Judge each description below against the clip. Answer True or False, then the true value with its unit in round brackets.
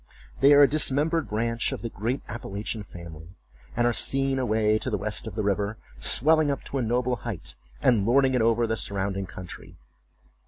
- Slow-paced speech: False (190 wpm)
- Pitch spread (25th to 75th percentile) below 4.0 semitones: False (4.5 semitones)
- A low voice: True (115 Hz)